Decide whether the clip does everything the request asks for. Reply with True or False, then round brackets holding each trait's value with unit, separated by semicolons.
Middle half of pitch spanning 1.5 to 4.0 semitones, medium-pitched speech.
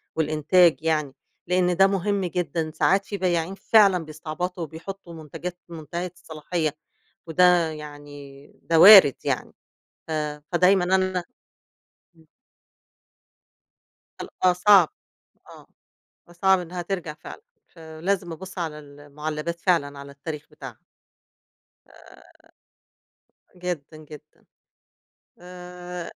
True (2.9 semitones; 170 Hz)